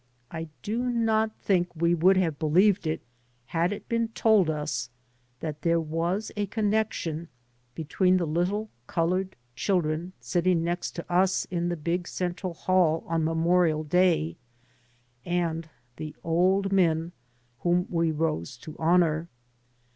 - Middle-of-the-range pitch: Yes, medium, 175 Hz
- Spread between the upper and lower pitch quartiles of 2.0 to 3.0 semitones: Yes, narrow, 2.5 semitones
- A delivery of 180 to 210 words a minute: No, slow, 135 wpm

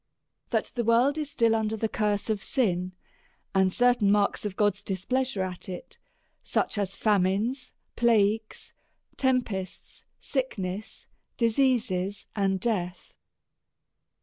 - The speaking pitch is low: No, high, 215 Hz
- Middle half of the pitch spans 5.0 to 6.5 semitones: No, average, 3.8 semitones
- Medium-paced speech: No, slow, 115 wpm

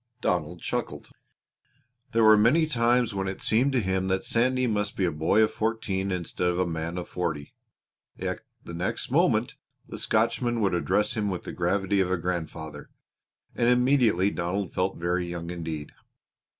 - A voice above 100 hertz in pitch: No, very low, 95 Hz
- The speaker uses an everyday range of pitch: Yes, average, 4.2 semitones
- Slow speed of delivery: No, average, 170 wpm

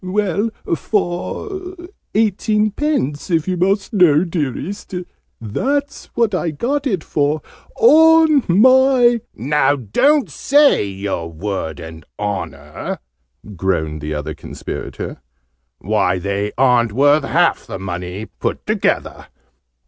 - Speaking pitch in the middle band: Yes, medium, 155 Hz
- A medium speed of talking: No, slow, 110 wpm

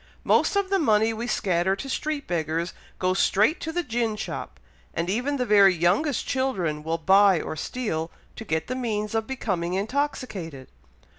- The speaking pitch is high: Yes, high, 210 Hz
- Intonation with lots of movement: Yes, wide, 6.6 semitones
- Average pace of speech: Yes, average, 170 wpm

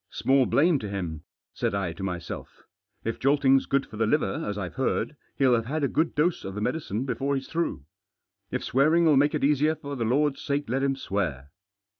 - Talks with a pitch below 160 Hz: Yes, low, 135 Hz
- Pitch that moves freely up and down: Yes, wide, 6.0 semitones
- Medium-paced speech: No, fast, 210 wpm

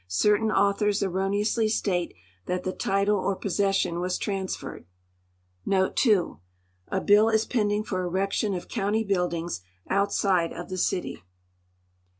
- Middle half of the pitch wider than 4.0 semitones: No, narrow, 2.6 semitones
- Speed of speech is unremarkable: No, slow, 125 wpm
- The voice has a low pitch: No, high, 195 Hz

